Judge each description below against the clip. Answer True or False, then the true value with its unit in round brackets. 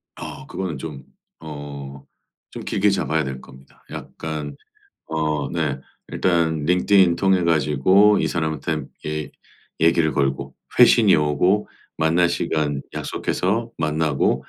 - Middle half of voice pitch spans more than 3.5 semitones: False (3.1 semitones)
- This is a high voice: False (80 Hz)